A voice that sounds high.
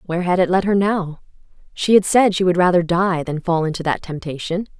No: medium, 180 Hz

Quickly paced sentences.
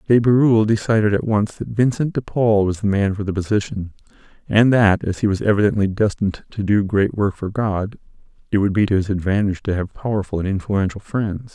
Yes: fast, 210 wpm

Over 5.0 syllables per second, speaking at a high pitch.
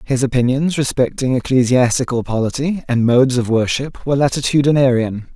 No: 5.6 syllables/s; low, 130 Hz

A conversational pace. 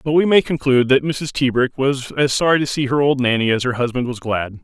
No: fast, 260 wpm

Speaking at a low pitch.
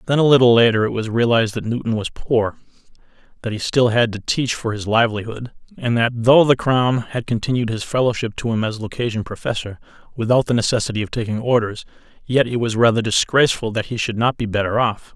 Yes: low, 115 Hz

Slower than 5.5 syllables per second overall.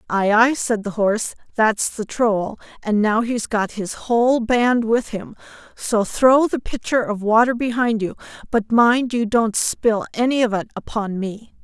Yes: 4.2 syllables/s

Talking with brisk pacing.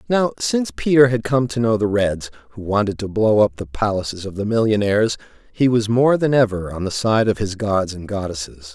Yes: fast, 220 wpm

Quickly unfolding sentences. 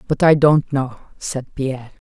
No: average, 175 wpm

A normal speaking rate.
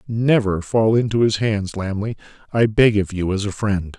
Yes: average, 195 wpm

